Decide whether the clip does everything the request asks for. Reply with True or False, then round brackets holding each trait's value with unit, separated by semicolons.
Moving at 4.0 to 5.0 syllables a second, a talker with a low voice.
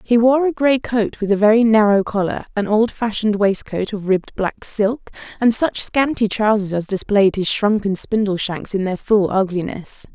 False (4.8 syllables/s; 210 Hz)